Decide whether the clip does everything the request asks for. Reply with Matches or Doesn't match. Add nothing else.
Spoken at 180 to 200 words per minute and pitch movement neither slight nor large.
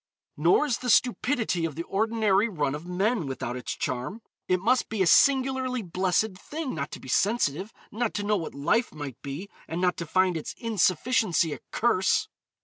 Doesn't match